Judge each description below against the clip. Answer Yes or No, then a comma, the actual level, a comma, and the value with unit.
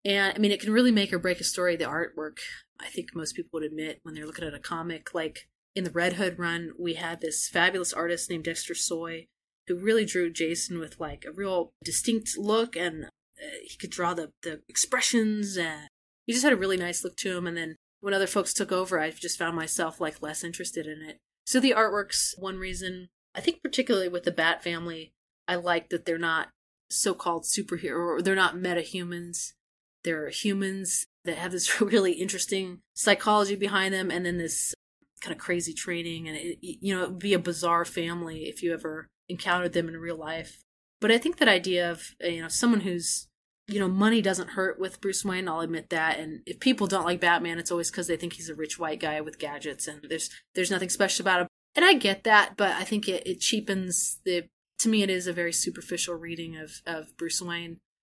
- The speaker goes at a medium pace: No, fast, 220 wpm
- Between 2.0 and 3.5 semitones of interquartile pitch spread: Yes, narrow, 2.6 semitones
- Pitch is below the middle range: No, medium, 175 Hz